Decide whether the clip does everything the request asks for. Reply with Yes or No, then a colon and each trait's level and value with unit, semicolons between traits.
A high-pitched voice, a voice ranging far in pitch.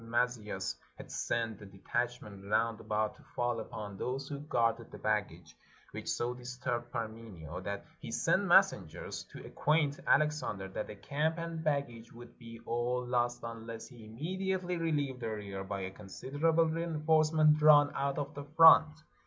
No: low, 120 Hz; wide, 5.7 semitones